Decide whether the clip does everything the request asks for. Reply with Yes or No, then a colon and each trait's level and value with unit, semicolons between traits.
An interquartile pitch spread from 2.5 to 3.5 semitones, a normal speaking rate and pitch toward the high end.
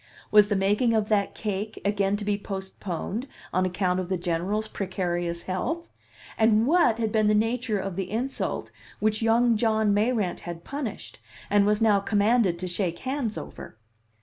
Yes: average, 2.9 semitones; average, 170 wpm; high, 210 Hz